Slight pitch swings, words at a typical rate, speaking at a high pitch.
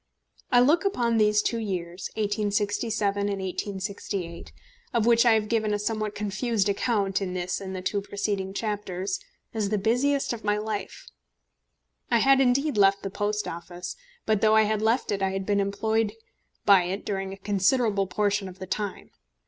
Yes: narrow, 2.2 semitones; average, 175 wpm; high, 205 Hz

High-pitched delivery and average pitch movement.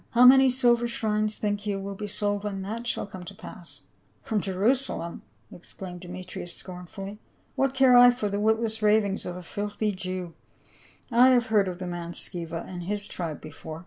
Yes: high, 205 Hz; average, 3.5 semitones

